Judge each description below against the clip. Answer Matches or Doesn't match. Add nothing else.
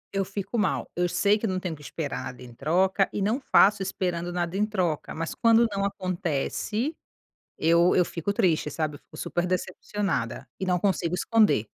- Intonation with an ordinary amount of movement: Matches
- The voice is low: Doesn't match